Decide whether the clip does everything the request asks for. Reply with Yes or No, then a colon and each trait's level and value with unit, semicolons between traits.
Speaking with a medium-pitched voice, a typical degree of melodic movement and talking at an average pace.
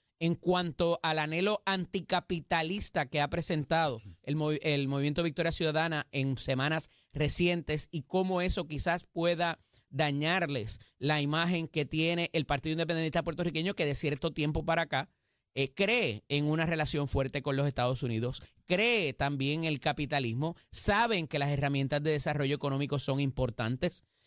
Yes: medium, 155 Hz; average, 3.1 semitones; average, 150 wpm